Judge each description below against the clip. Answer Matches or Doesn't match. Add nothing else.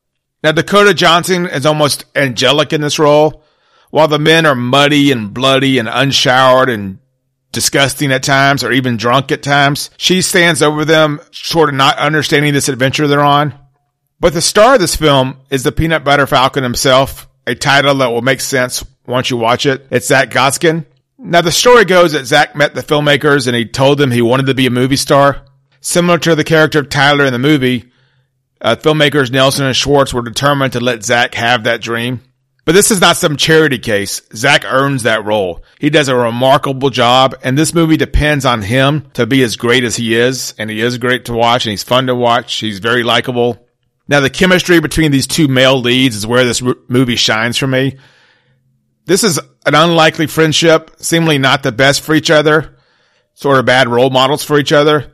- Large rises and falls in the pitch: Doesn't match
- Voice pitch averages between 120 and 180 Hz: Matches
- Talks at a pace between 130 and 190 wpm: Doesn't match